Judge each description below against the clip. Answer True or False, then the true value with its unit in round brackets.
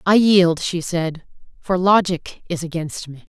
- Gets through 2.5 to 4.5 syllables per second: True (4.0 syllables/s)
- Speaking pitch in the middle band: True (175 Hz)